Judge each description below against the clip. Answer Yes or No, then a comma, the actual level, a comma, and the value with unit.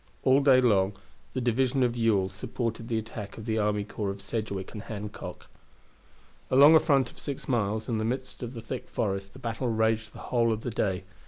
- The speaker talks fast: Yes, fast, 210 wpm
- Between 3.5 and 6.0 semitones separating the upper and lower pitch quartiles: No, average, 3.1 semitones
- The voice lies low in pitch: Yes, low, 115 Hz